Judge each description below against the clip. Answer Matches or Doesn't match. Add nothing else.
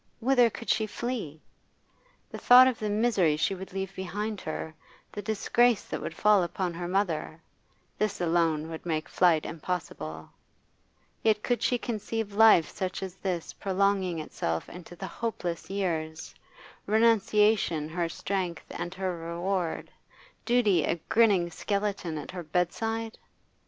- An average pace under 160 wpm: Matches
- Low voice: Doesn't match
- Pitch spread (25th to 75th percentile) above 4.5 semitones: Doesn't match